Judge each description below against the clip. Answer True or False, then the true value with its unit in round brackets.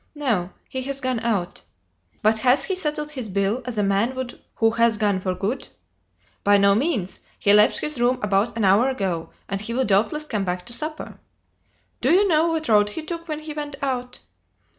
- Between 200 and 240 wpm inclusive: True (205 wpm)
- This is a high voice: True (235 Hz)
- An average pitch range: False (6.3 semitones)